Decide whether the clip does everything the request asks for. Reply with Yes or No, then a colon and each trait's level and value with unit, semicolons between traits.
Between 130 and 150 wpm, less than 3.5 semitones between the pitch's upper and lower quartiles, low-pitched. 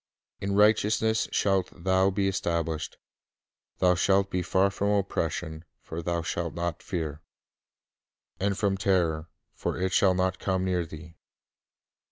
Yes: average, 140 wpm; narrow, 2.6 semitones; very low, 95 Hz